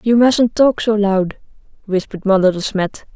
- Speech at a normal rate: Yes, average, 170 wpm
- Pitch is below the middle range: No, high, 210 Hz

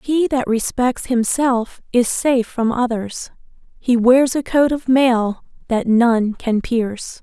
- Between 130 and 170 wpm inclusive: Yes, average, 150 wpm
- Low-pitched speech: No, high, 245 Hz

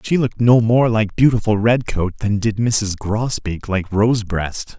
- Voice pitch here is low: Yes, low, 110 Hz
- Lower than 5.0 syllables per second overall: Yes, 4.4 syllables/s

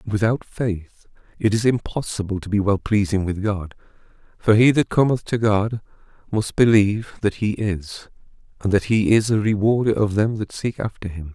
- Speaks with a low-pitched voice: Yes, low, 105 Hz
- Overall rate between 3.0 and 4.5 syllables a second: No, 5.0 syllables/s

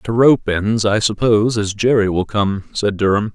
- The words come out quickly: No, average, 195 wpm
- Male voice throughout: Yes, male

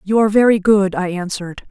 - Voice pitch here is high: Yes, high, 200 Hz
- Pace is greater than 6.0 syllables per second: Yes, 6.3 syllables/s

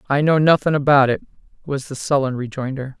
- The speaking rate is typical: Yes, average, 180 wpm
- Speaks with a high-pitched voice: No, medium, 140 Hz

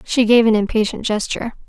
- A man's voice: No, female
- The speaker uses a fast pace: No, average, 180 wpm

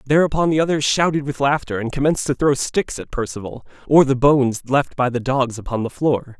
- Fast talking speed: Yes, fast, 215 wpm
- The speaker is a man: Yes, male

